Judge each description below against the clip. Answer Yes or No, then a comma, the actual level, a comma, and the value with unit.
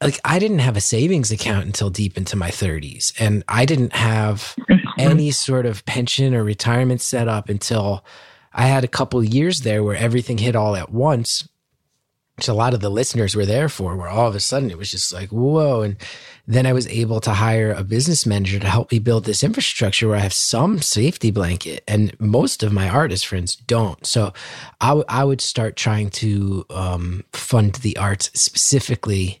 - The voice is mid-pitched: No, low, 115 Hz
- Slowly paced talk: No, average, 200 wpm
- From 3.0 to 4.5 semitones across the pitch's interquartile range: Yes, average, 4.1 semitones